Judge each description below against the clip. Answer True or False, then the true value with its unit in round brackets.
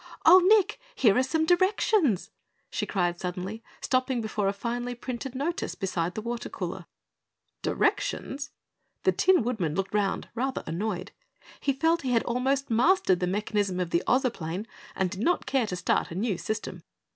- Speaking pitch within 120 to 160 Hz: False (235 Hz)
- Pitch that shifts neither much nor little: False (6.0 semitones)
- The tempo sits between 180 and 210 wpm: False (165 wpm)